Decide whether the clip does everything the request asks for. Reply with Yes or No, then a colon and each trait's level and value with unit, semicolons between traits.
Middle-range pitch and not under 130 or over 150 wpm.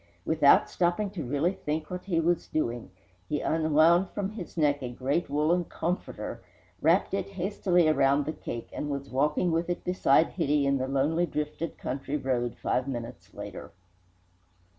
No: medium, 155 Hz; average, 160 wpm